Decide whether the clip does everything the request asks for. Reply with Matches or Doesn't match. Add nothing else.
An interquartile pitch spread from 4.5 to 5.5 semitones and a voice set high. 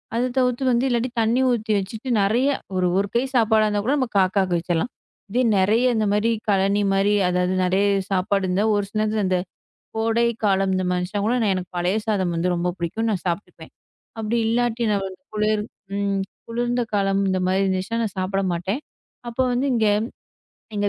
Doesn't match